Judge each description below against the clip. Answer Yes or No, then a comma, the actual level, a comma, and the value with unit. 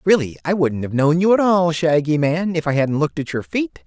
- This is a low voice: No, medium, 155 Hz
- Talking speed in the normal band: No, fast, 265 wpm